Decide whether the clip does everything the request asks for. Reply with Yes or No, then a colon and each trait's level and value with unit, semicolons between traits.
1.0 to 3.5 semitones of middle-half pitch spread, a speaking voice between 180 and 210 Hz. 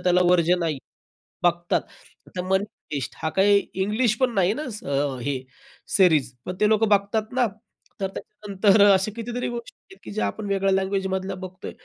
Yes: average, 2.8 semitones; high, 195 Hz